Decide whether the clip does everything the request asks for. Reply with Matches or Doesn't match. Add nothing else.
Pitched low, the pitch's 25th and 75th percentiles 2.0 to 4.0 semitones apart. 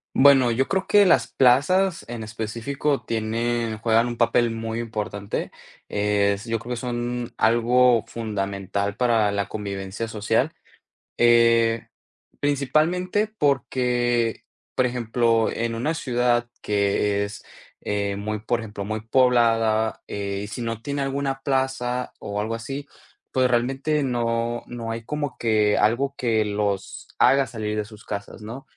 Matches